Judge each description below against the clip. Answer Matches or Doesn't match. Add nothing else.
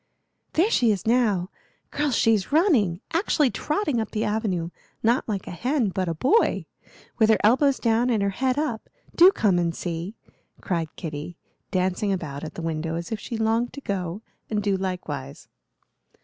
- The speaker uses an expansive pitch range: Matches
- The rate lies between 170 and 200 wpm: Matches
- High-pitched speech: Matches